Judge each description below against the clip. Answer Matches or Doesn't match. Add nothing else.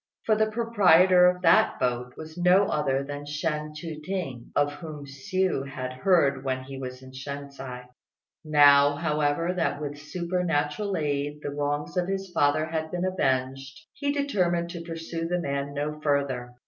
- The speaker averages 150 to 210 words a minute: Matches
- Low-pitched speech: Doesn't match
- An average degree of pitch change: Matches